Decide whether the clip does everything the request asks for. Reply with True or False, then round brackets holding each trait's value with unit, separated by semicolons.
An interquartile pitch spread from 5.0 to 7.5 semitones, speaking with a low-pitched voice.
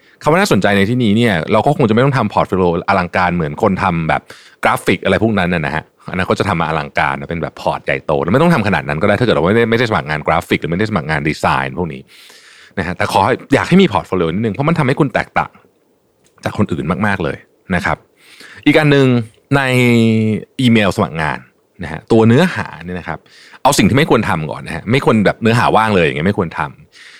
True (5.6 semitones; 105 Hz)